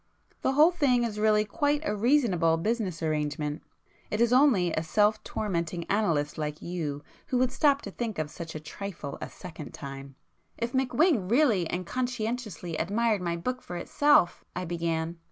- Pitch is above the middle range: Yes, high, 200 Hz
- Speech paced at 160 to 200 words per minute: Yes, average, 165 wpm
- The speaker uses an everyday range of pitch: No, wide, 6.8 semitones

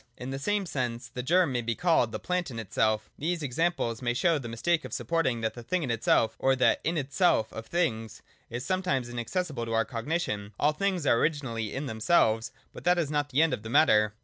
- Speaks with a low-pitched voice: Yes, low, 130 Hz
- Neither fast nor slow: No, fast, 225 wpm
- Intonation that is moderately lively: No, wide, 6.4 semitones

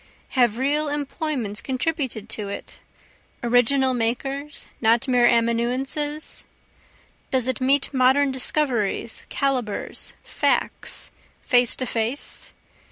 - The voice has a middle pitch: No, very high, 255 Hz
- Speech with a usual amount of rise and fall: Yes, average, 3.1 semitones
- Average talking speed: No, slow, 100 wpm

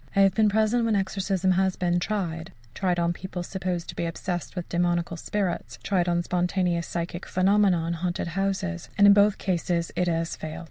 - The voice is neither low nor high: Yes, medium, 180 Hz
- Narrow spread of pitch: Yes, narrow, 2.2 semitones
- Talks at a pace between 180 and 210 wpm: Yes, average, 195 wpm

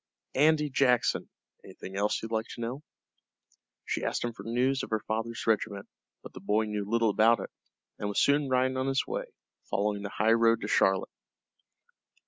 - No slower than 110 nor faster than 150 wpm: No, average, 175 wpm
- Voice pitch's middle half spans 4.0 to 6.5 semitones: No, average, 3.6 semitones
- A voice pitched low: Yes, low, 115 Hz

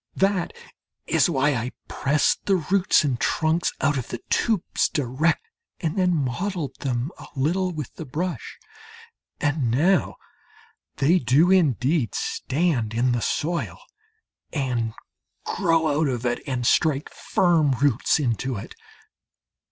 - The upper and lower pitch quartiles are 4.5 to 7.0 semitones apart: Yes, average, 5.1 semitones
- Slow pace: Yes, slow, 130 wpm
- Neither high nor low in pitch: Yes, medium, 145 Hz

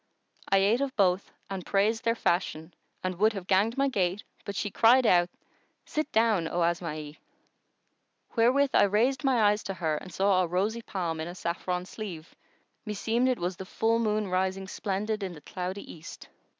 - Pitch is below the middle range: No, high, 195 Hz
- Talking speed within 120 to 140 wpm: No, average, 180 wpm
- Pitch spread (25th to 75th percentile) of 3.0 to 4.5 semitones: Yes, average, 3.8 semitones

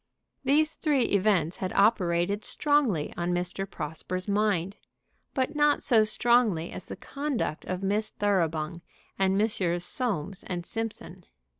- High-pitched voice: Yes, high, 200 Hz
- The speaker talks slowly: Yes, slow, 130 wpm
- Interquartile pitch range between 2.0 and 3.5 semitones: No, average, 4.8 semitones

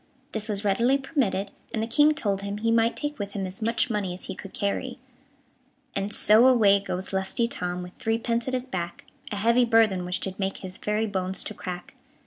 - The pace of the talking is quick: Yes, fast, 215 wpm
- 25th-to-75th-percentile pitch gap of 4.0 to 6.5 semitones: No, average, 3.4 semitones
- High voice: Yes, high, 210 Hz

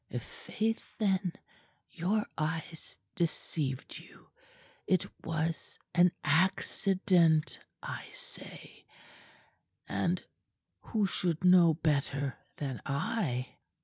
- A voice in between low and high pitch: Yes, medium, 165 Hz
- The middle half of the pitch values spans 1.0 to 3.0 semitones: No, average, 3.6 semitones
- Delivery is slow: Yes, slow, 80 wpm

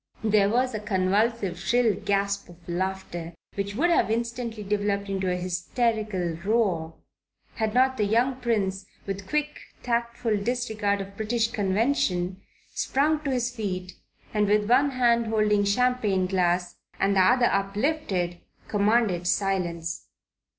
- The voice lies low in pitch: No, high, 205 Hz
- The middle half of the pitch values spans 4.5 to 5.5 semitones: No, average, 3.8 semitones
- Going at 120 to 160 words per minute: Yes, slow, 135 wpm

